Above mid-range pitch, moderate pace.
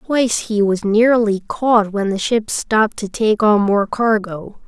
Yes: high, 215 Hz; average, 180 wpm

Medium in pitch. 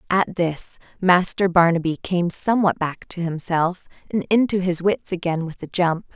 Yes: medium, 175 Hz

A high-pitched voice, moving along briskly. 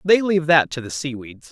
No: medium, 155 Hz; fast, 240 wpm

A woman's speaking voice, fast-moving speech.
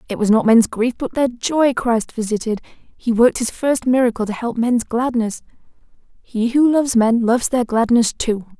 No: female; average, 190 wpm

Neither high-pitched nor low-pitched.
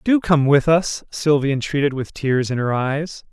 Yes: medium, 145 Hz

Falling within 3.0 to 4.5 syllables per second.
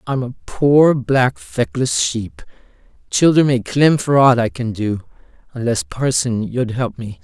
Yes: 3.8 syllables/s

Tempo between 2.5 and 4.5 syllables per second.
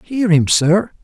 Yes: 3.2 syllables/s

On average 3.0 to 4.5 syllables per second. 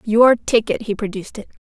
No: 5.7 syllables/s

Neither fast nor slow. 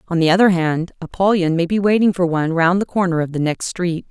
No: fast, 250 wpm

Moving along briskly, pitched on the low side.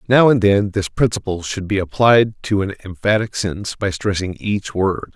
No: average, 185 wpm; low, 100 Hz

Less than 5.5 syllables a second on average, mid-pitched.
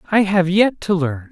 Yes: 4.7 syllables/s; medium, 180 Hz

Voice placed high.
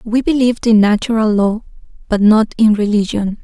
Yes: high, 220 Hz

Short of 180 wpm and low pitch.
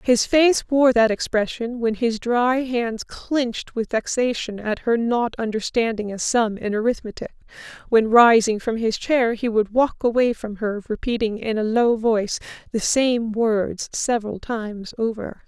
No: average, 165 wpm; high, 230 Hz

